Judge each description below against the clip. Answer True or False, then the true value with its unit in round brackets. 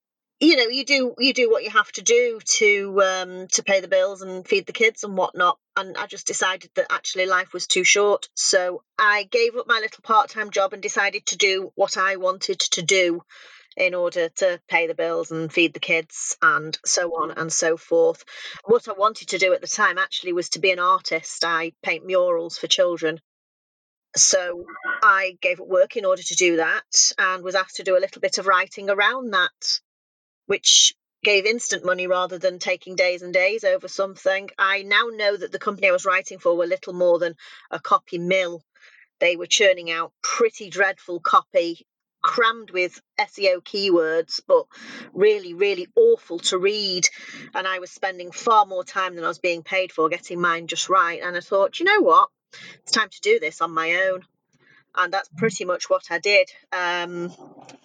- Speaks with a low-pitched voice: False (190 Hz)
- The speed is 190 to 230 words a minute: True (200 wpm)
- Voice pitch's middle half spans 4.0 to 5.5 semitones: True (4.5 semitones)